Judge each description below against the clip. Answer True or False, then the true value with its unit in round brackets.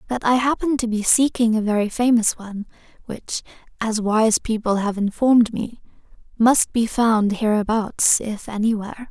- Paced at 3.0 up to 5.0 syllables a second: True (4.7 syllables/s)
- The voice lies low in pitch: False (225 Hz)